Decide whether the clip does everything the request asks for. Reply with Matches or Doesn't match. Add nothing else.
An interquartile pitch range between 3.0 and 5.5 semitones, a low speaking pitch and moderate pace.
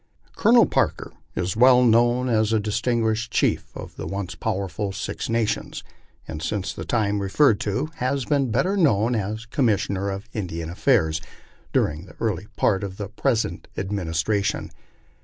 Matches